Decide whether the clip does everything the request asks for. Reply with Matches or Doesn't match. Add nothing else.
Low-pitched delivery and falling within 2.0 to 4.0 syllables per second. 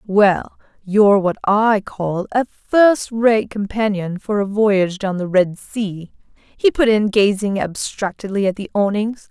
Doesn't match